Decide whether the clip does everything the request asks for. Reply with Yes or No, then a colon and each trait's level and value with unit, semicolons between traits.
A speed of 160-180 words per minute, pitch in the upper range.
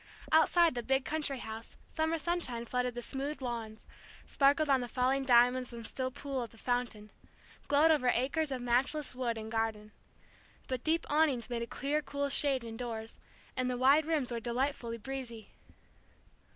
Yes: average, 165 wpm; very high, 255 Hz